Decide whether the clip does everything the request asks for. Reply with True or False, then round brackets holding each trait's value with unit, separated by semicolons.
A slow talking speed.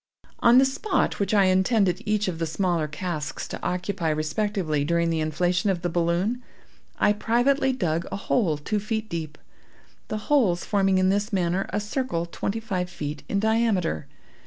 False (170 wpm)